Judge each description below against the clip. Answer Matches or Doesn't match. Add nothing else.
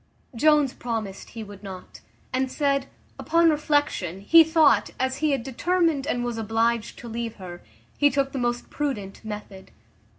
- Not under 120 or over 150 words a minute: Doesn't match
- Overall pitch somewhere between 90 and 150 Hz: Doesn't match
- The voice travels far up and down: Doesn't match